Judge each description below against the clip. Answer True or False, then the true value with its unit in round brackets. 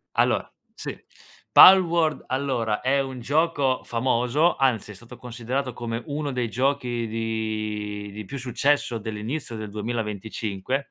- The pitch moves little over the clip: False (3.8 semitones)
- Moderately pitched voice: False (120 Hz)